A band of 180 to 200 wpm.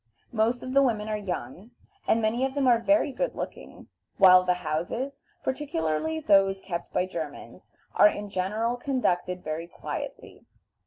No: average, 155 wpm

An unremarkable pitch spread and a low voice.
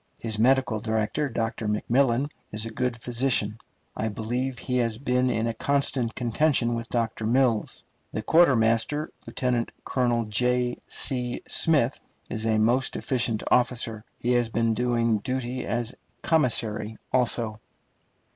No: narrow, 2.2 semitones; low, 120 Hz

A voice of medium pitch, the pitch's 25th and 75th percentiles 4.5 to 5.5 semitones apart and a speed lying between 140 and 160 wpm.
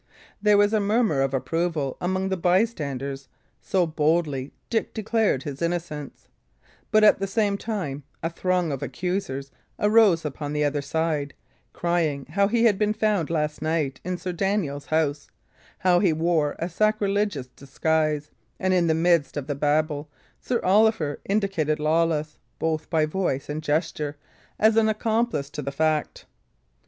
Yes: medium, 165 Hz; average, 5.0 semitones; average, 150 wpm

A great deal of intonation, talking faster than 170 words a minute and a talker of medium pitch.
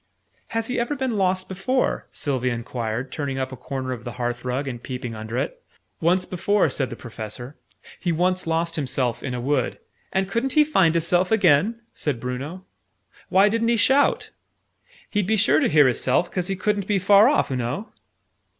Yes: wide, 7.8 semitones; average, 195 wpm; medium, 165 Hz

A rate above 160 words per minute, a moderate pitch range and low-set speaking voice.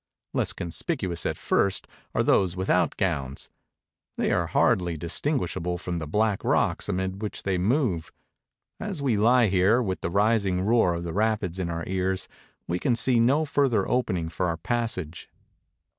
Yes: average, 170 wpm; average, 4.9 semitones; very low, 95 Hz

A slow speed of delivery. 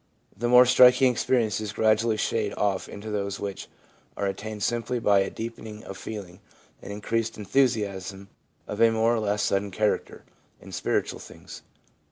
No: average, 155 wpm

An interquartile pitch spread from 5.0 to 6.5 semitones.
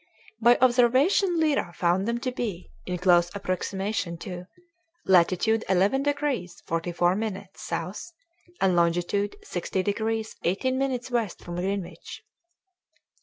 Yes: wide, 5.4 semitones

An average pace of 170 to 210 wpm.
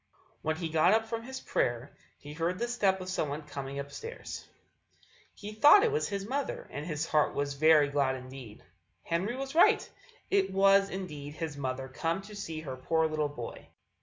Yes: average, 190 wpm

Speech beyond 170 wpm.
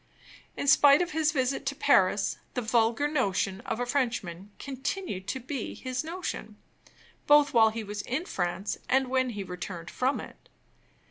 No: average, 160 wpm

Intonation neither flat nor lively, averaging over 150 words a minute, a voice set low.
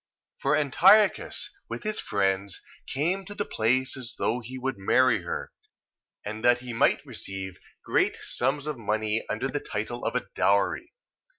No: wide, 5.8 semitones; average, 160 wpm; low, 125 Hz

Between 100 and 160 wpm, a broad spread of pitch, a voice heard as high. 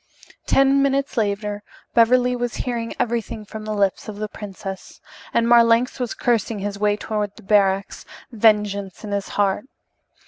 No: average, 150 wpm; narrow, 2.6 semitones; high, 215 Hz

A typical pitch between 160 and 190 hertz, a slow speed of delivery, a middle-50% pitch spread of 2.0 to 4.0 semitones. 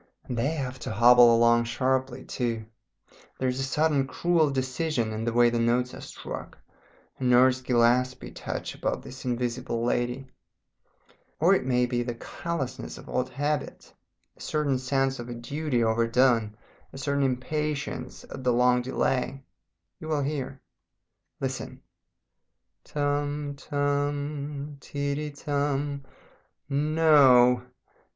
No: low, 130 Hz; slow, 130 wpm; average, 2.8 semitones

